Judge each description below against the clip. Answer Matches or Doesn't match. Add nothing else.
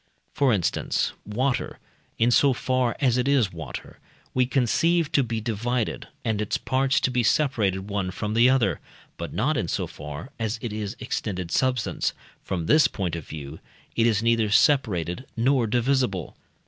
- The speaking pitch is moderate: Doesn't match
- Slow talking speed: Doesn't match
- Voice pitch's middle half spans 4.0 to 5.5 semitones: Matches